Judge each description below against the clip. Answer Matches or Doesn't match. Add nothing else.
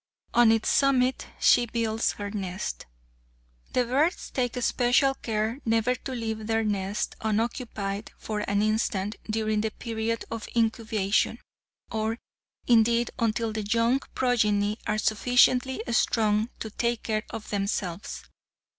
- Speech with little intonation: Matches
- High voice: Matches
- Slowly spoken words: Matches